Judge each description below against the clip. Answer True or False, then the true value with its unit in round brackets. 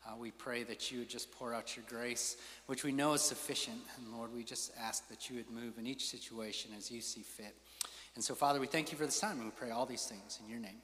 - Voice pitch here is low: True (120 Hz)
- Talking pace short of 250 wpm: False (275 wpm)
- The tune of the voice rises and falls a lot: False (2.9 semitones)